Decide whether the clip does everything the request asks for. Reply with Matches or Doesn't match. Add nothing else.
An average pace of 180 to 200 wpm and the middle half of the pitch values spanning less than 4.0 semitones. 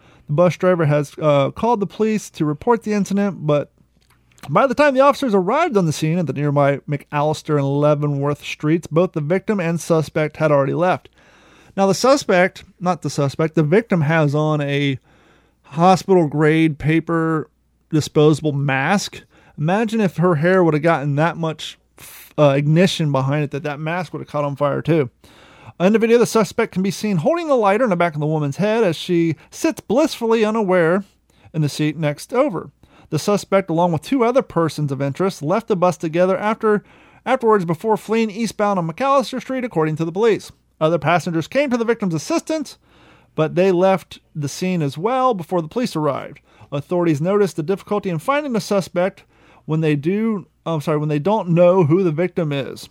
Doesn't match